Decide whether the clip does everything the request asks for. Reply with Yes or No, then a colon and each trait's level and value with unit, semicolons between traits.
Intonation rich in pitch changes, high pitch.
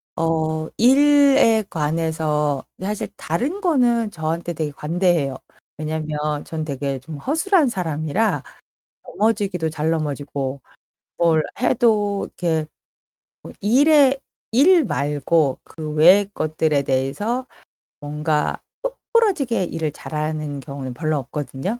No: wide, 7.0 semitones; medium, 160 Hz